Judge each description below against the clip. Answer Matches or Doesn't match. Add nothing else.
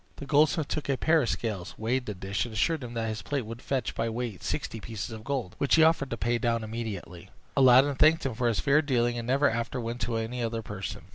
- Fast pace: Matches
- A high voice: Doesn't match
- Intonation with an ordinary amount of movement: Matches